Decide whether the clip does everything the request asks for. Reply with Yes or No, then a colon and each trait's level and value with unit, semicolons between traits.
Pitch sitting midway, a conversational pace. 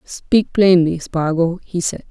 Yes: medium, 175 Hz; average, 145 wpm